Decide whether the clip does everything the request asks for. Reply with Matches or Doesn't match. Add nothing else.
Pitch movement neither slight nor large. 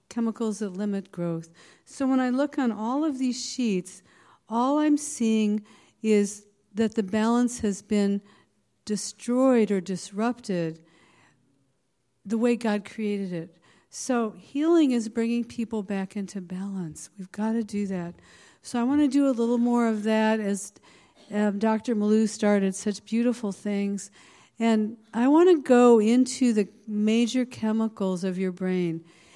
Matches